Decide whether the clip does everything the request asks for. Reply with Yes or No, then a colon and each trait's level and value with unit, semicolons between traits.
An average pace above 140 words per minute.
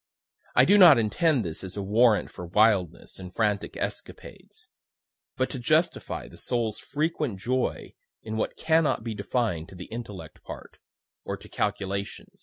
Yes: average, 155 wpm